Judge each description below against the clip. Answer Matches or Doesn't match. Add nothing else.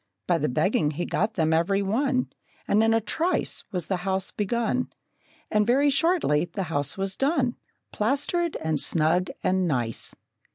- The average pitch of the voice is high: Matches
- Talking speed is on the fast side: Doesn't match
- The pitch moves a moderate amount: Doesn't match